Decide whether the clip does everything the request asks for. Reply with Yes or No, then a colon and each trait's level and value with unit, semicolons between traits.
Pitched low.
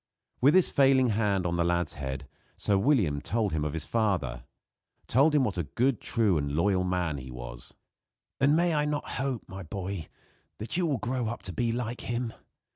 Yes: low, 105 Hz